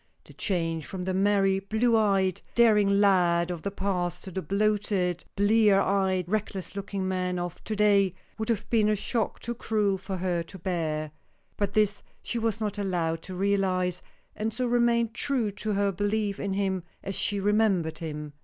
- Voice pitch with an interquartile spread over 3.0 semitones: No, narrow, 2.6 semitones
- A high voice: Yes, high, 195 Hz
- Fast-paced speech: No, average, 180 wpm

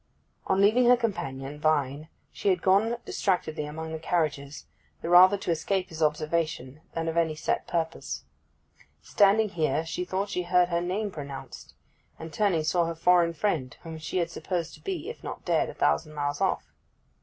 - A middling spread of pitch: Yes, average, 3.5 semitones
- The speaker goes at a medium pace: Yes, average, 180 wpm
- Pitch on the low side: No, medium, 170 Hz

